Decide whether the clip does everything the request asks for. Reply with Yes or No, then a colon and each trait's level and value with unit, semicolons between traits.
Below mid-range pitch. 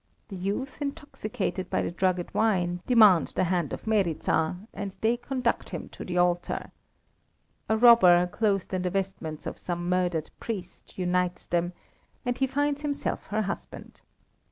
No: high, 190 Hz